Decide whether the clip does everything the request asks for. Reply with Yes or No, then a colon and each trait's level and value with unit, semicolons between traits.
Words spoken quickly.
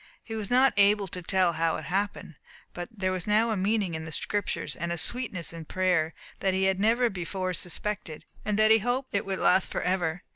Yes: fast, 220 wpm